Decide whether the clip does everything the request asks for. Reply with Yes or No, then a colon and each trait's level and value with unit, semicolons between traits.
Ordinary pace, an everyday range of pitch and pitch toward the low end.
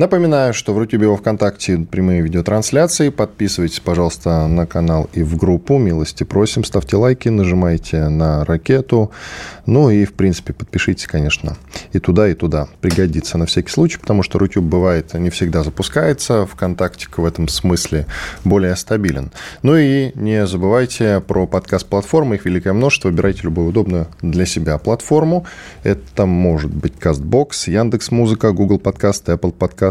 Yes: average, 145 wpm; average, 4.2 semitones; very low, 95 Hz